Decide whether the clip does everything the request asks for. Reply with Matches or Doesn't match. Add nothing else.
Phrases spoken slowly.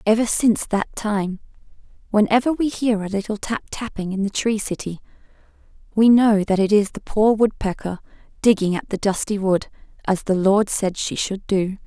Doesn't match